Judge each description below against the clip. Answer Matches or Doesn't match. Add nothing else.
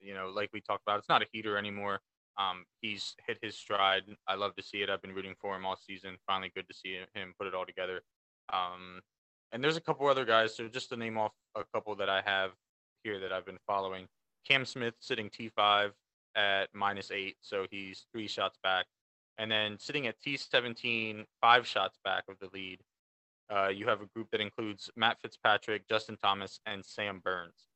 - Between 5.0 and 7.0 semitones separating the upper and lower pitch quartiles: Doesn't match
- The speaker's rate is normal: Doesn't match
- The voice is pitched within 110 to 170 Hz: Doesn't match